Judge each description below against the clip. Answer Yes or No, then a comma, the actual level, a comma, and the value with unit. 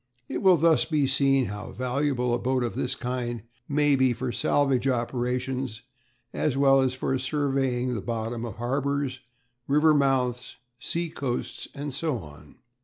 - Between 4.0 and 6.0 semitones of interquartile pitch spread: No, narrow, 2.5 semitones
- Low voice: Yes, low, 130 Hz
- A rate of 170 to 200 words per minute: No, average, 155 wpm